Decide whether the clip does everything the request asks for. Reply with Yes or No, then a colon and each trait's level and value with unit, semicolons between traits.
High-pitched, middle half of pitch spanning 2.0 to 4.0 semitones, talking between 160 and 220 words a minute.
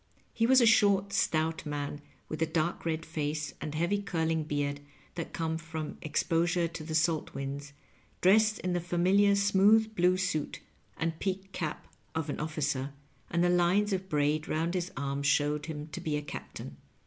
No: medium, 165 Hz; average, 3.6 semitones; average, 175 wpm